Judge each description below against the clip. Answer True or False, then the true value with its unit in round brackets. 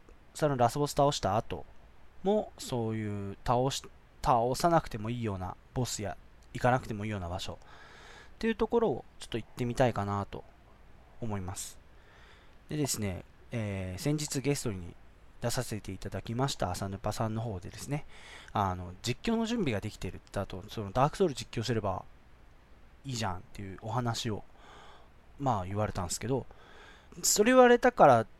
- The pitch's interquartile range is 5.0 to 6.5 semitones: True (5.3 semitones)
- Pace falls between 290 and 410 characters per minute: True (335 characters per minute)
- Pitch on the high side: False (110 Hz)